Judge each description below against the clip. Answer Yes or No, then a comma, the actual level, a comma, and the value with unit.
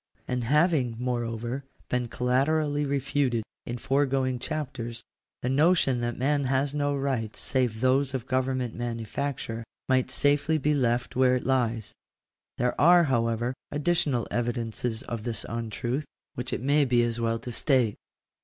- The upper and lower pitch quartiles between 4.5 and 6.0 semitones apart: No, average, 2.9 semitones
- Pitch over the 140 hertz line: No, low, 130 Hz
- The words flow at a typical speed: Yes, average, 145 wpm